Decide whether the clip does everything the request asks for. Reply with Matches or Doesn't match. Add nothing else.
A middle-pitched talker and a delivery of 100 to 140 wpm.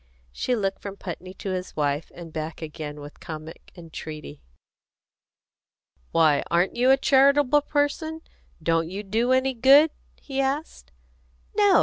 Doesn't match